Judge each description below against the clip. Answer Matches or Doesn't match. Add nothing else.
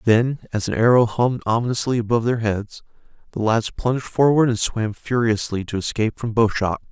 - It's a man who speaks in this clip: Matches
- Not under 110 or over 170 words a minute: Doesn't match